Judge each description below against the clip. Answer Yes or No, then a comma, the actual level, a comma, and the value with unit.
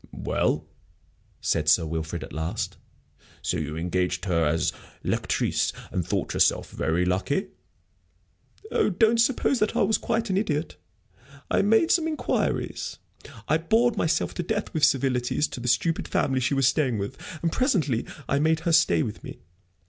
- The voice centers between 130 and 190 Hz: Yes, medium, 140 Hz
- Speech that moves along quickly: No, average, 160 wpm